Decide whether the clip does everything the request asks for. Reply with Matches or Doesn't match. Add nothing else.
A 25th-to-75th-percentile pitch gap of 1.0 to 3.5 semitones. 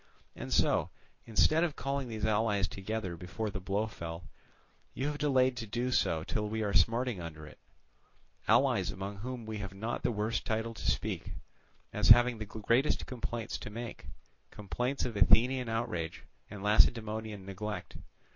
Matches